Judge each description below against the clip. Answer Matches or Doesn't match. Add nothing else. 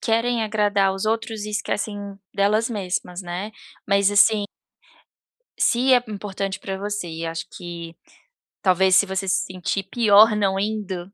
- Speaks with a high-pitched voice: Matches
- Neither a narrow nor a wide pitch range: Doesn't match